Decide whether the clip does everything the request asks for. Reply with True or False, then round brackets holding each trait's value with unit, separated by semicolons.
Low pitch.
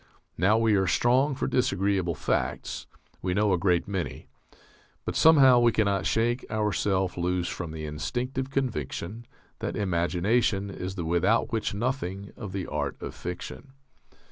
True (100 Hz)